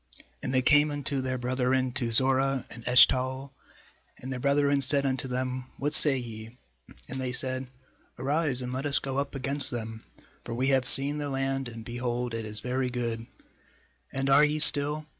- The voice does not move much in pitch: Yes, narrow, 1.9 semitones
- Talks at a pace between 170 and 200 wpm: Yes, average, 180 wpm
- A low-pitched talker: Yes, low, 130 Hz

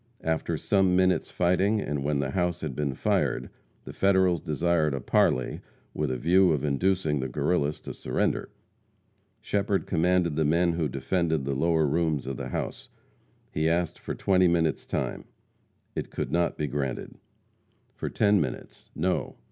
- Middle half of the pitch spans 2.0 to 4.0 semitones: Yes, average, 3.6 semitones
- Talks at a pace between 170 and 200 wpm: No, average, 160 wpm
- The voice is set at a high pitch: No, very low, 80 Hz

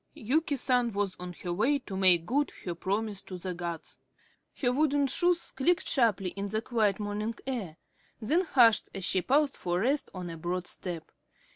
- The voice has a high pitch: Yes, high, 210 Hz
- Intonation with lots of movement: Yes, wide, 6.5 semitones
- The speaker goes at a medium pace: Yes, average, 180 wpm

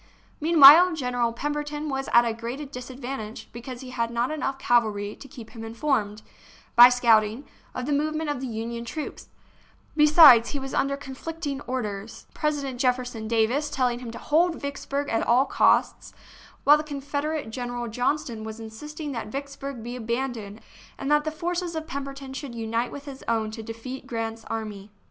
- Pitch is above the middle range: Yes, very high, 255 Hz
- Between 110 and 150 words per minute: No, average, 175 wpm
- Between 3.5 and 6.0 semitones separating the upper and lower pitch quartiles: Yes, average, 3.9 semitones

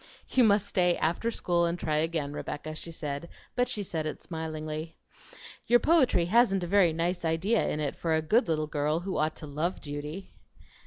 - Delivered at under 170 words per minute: No, average, 195 wpm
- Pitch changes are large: No, average, 3.6 semitones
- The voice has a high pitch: No, medium, 165 Hz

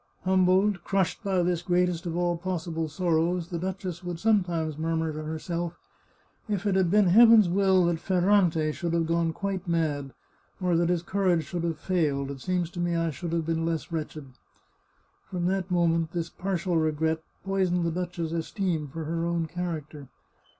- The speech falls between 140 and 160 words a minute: No, average, 185 wpm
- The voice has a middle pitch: Yes, medium, 170 Hz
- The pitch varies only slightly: Yes, narrow, 2.0 semitones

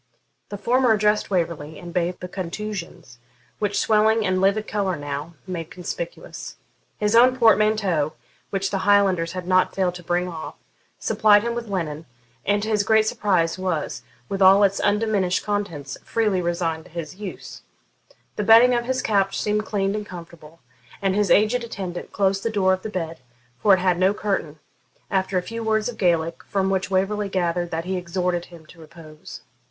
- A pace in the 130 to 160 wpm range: No, average, 180 wpm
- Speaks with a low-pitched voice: No, high, 190 Hz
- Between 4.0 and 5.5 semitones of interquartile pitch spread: No, average, 3.4 semitones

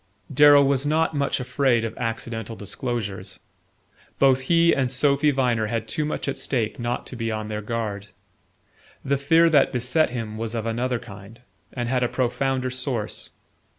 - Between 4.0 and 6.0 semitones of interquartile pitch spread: No, average, 3.4 semitones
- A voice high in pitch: No, low, 125 Hz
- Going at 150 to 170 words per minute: Yes, average, 165 wpm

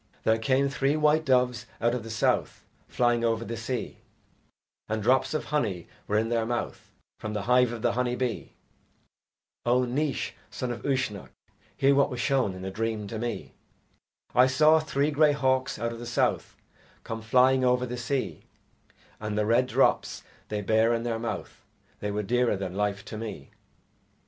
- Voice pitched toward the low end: Yes, low, 120 Hz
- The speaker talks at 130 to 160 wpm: No, average, 180 wpm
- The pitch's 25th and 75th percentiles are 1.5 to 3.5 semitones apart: Yes, average, 2.8 semitones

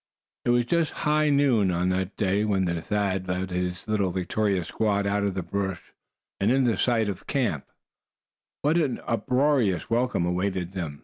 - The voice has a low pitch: Yes, low, 100 Hz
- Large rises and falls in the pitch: No, average, 4.8 semitones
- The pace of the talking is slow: No, average, 170 wpm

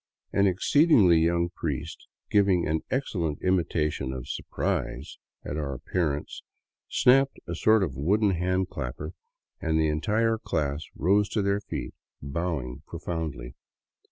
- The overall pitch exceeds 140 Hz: No, very low, 85 Hz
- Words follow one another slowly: Yes, slow, 125 wpm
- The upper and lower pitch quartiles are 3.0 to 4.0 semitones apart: No, average, 4.7 semitones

